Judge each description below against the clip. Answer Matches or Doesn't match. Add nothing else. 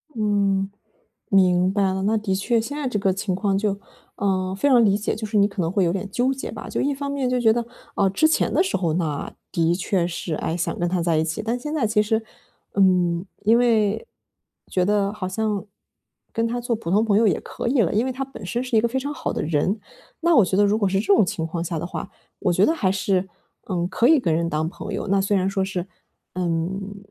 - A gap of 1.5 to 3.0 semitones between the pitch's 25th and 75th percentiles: Doesn't match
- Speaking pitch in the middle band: Doesn't match